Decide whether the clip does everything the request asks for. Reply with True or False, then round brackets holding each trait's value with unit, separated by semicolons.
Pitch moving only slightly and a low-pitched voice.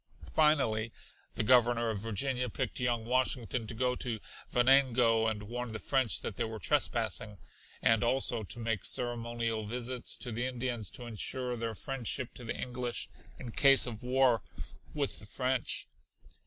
True (2.1 semitones; 120 Hz)